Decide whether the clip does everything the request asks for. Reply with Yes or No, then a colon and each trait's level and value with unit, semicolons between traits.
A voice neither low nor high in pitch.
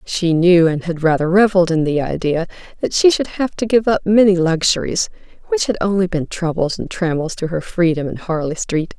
Yes: medium, 180 Hz